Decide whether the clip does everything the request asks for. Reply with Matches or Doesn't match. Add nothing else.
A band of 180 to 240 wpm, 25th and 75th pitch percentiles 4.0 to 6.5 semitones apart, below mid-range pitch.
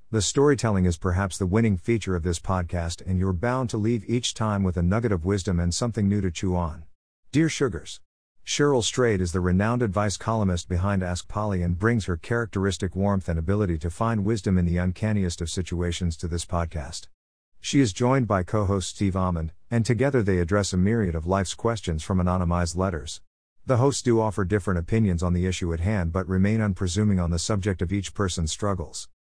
Doesn't match